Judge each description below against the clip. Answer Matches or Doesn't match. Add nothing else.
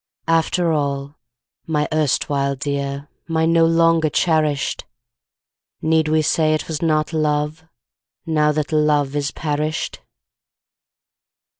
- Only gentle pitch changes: Matches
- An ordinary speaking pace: Doesn't match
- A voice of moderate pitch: Matches